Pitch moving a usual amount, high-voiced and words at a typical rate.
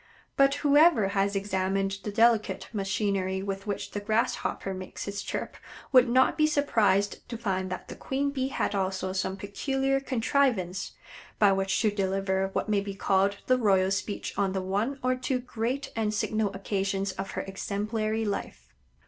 Yes: average, 3.5 semitones; high, 200 Hz; average, 170 wpm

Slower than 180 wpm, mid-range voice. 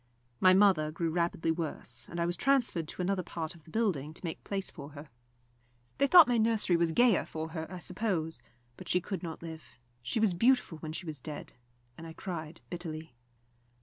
No: average, 200 wpm; medium, 170 Hz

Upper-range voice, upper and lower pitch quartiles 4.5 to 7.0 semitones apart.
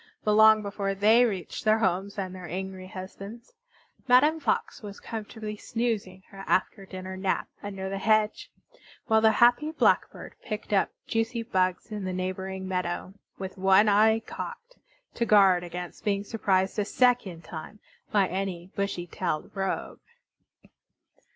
No: high, 200 Hz; average, 2.7 semitones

